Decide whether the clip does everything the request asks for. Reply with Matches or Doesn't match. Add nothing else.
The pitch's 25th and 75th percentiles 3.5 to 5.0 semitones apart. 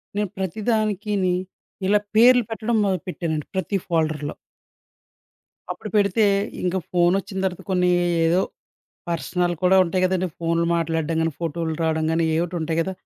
Doesn't match